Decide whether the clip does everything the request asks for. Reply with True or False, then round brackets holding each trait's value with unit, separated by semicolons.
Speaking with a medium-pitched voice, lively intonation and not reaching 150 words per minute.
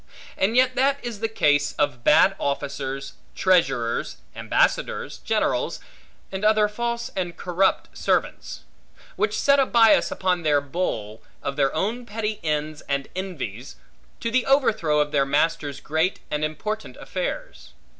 True (175 Hz; 7.4 semitones; 140 wpm)